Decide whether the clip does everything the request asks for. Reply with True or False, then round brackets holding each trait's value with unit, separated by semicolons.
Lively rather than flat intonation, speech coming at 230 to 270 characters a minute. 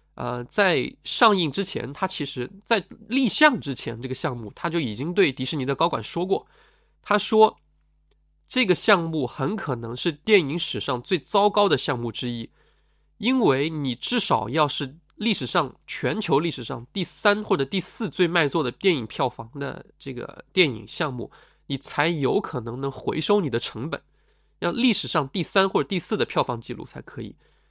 True (7.2 semitones; 260 characters per minute)